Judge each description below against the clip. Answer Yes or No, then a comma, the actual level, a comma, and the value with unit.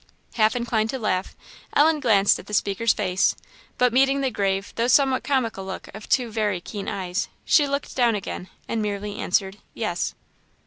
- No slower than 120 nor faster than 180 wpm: Yes, average, 175 wpm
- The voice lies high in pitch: Yes, high, 220 Hz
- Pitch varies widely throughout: No, average, 4.1 semitones